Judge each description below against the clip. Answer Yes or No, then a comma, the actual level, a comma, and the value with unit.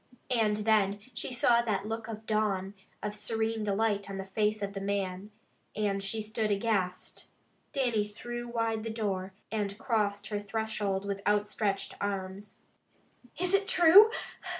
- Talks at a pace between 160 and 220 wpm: No, average, 150 wpm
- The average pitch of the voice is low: No, high, 210 Hz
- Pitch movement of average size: No, narrow, 2.1 semitones